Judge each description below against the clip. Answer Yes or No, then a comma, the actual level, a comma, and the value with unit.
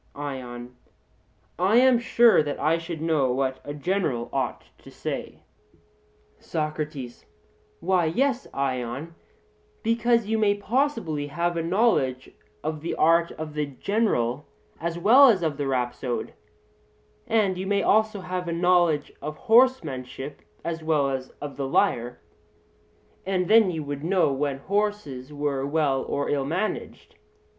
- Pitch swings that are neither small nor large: No, wide, 6.2 semitones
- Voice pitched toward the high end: No, medium, 160 Hz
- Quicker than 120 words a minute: Yes, average, 140 wpm